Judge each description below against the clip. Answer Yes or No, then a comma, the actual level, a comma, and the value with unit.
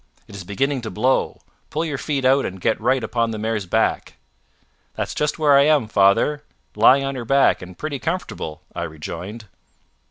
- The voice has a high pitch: No, low, 120 Hz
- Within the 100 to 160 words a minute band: No, average, 185 wpm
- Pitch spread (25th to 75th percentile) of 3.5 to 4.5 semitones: No, wide, 5.5 semitones